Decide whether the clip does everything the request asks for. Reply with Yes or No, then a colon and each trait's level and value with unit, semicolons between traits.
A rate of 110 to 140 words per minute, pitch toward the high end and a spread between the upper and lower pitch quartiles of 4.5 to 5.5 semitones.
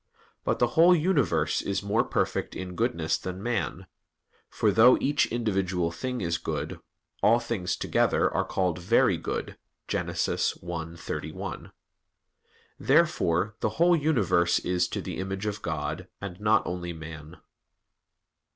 No: slow, 135 wpm; very low, 95 Hz; average, 5.2 semitones